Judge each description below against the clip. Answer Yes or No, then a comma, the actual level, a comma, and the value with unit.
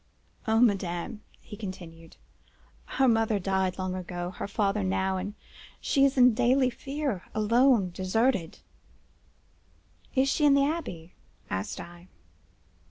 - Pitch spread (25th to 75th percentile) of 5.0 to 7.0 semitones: Yes, wide, 5.4 semitones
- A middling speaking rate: No, slow, 110 wpm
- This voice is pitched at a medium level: No, high, 205 Hz